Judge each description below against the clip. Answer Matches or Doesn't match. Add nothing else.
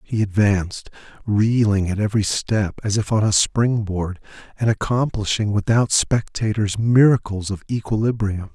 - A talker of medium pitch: Doesn't match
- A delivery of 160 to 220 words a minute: Doesn't match